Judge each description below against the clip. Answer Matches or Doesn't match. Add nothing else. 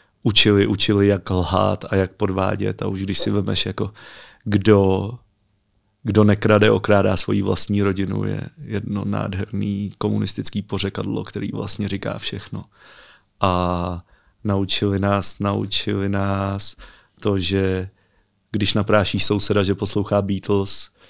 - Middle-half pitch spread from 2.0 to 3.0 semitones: Doesn't match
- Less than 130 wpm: Matches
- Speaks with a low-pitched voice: Matches